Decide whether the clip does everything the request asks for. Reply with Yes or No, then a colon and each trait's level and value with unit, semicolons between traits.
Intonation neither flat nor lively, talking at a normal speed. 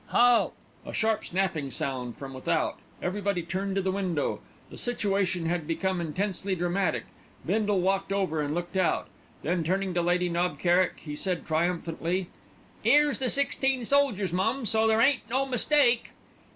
Yes: average, 4.1 semitones; average, 155 wpm